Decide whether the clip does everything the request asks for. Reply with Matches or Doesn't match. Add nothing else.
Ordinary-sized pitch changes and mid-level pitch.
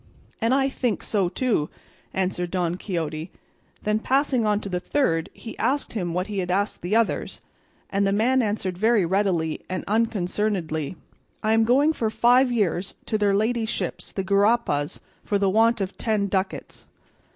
Doesn't match